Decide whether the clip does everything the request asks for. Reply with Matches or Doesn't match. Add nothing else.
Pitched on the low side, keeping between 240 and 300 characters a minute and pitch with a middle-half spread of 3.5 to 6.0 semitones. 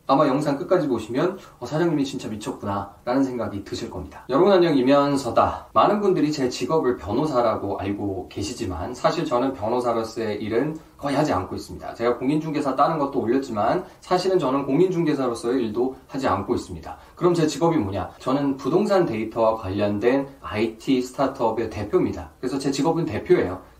Doesn't match